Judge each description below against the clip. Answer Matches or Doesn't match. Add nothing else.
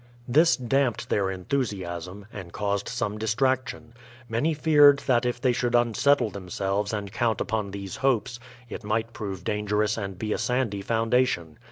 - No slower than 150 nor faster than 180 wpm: Matches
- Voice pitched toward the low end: Matches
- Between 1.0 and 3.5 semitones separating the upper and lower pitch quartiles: Doesn't match